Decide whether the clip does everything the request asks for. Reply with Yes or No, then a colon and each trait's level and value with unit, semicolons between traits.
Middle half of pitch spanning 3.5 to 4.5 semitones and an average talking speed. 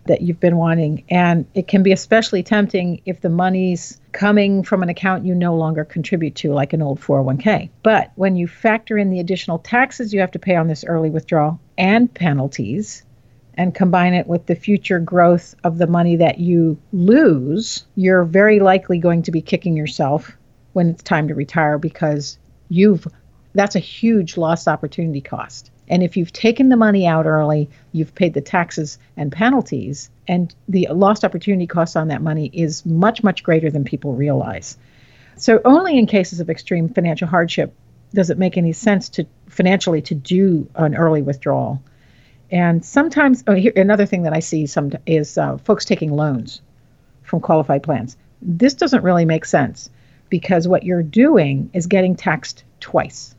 Yes: average, 3.8 semitones; average, 180 wpm